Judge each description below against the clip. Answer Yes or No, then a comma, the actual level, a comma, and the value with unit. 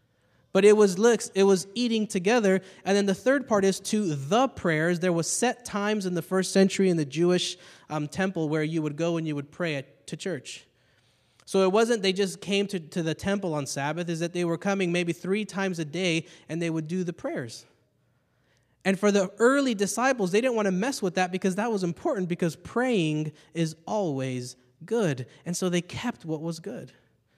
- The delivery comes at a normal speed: No, fast, 210 wpm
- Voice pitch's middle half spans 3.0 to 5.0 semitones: Yes, average, 3.6 semitones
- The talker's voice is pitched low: No, medium, 185 Hz